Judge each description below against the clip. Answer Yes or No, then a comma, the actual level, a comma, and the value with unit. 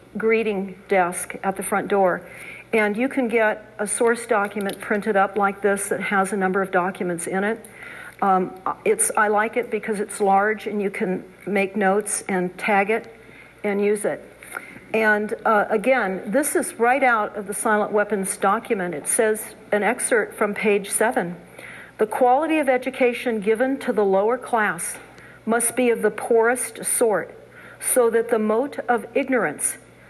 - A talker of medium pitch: No, high, 215 Hz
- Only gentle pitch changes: No, average, 3.1 semitones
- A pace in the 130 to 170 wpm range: Yes, average, 165 wpm